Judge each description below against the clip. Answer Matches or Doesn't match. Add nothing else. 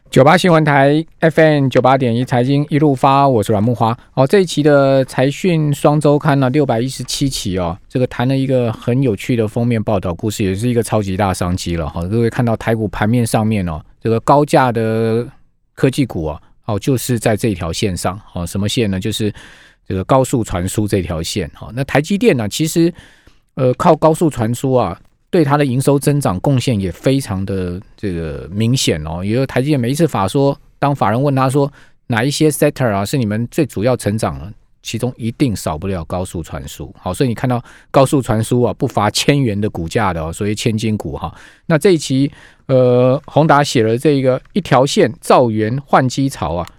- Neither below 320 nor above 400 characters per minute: Doesn't match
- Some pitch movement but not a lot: Matches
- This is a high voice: Doesn't match